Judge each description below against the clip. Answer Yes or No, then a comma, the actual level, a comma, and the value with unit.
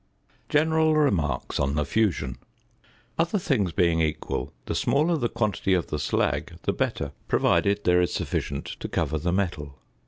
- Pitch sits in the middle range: No, very low, 95 Hz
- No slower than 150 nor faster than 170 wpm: Yes, average, 155 wpm